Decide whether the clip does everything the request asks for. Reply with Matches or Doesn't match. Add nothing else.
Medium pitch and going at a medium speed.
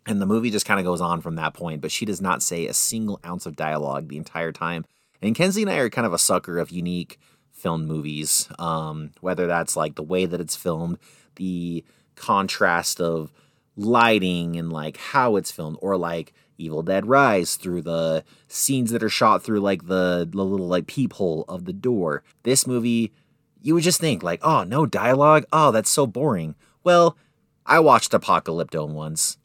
Doesn't match